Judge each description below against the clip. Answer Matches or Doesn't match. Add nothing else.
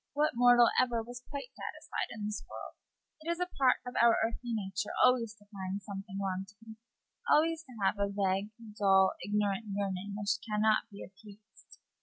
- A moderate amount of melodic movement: Matches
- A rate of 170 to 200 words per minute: Matches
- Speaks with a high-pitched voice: Matches